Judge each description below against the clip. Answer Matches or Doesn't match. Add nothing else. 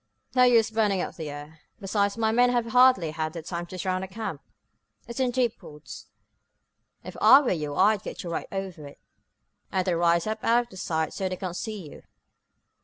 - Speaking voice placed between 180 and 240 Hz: Matches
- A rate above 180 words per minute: Matches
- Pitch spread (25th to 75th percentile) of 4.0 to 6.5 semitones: Matches